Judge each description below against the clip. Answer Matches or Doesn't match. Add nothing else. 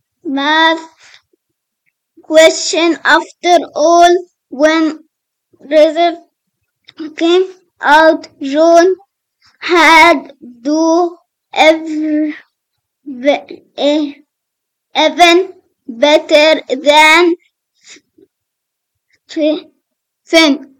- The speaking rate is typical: Doesn't match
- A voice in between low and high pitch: Doesn't match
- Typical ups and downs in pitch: Doesn't match